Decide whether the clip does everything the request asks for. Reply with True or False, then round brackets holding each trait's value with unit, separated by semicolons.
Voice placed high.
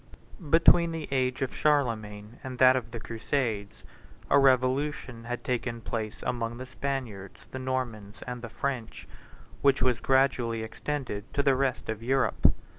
False (125 Hz)